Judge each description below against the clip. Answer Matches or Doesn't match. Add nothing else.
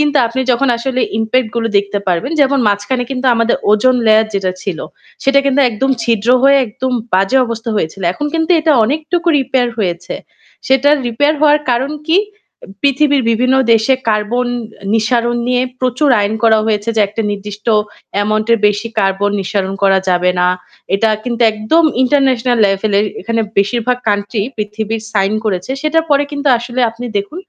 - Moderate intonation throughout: Matches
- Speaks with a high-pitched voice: Matches